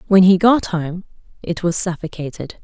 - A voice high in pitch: No, medium, 180 Hz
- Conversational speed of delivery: Yes, average, 160 wpm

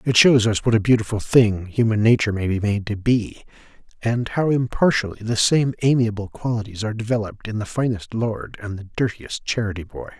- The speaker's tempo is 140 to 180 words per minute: No, average, 190 wpm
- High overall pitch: No, low, 110 Hz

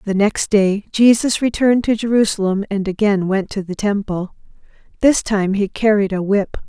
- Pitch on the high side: Yes, high, 205 Hz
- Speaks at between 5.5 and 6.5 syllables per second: No, 4.9 syllables/s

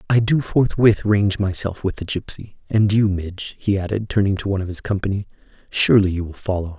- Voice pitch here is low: Yes, low, 100 Hz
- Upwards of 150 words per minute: Yes, fast, 205 wpm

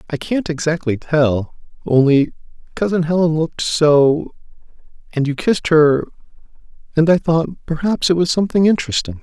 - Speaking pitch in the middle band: Yes, medium, 160 Hz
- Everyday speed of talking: No, slow, 115 wpm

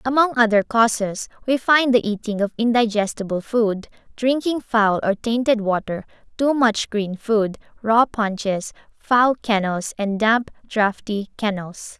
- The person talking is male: No, female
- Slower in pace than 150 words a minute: Yes, slow, 135 wpm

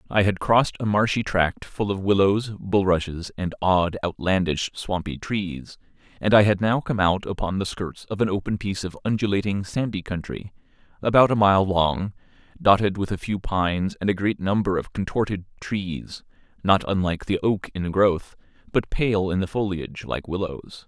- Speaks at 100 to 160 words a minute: No, average, 175 wpm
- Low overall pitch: Yes, very low, 95 Hz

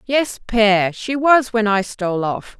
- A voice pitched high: Yes, high, 220 Hz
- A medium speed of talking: Yes, average, 185 wpm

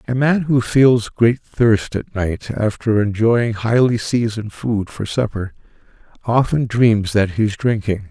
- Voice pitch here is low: Yes, low, 110 Hz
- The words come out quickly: No, average, 155 wpm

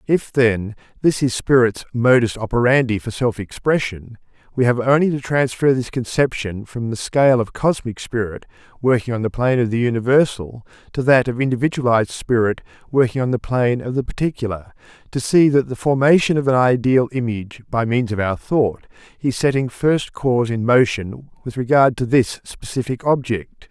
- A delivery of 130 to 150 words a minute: No, average, 170 wpm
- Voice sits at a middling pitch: No, low, 120 Hz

